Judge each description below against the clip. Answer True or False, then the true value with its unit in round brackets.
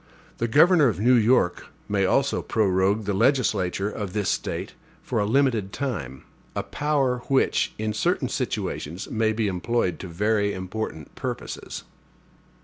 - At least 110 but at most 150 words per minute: True (140 wpm)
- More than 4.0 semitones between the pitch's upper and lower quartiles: True (4.7 semitones)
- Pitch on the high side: False (105 Hz)